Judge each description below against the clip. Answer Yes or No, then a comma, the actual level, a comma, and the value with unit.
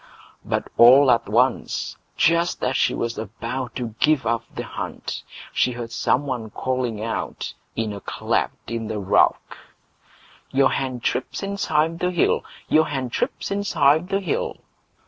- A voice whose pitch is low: Yes, low, 130 Hz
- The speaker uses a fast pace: No, average, 150 wpm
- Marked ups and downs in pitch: No, average, 4.9 semitones